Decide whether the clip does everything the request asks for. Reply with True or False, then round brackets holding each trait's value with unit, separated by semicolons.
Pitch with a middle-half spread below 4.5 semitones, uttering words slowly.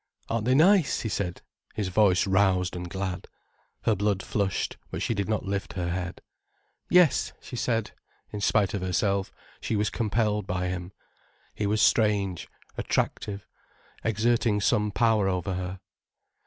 False (2.7 semitones; 150 wpm)